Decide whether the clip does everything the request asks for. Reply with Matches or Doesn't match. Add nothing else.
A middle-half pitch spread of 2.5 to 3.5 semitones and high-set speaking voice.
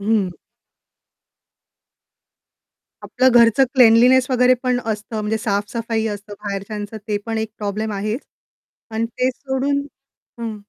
Matches